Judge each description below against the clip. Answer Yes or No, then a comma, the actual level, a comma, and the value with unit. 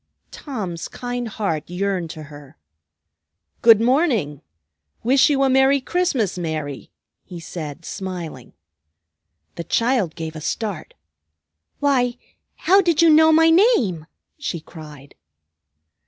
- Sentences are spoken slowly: Yes, slow, 115 wpm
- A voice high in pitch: Yes, high, 200 Hz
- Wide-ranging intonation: Yes, wide, 8.9 semitones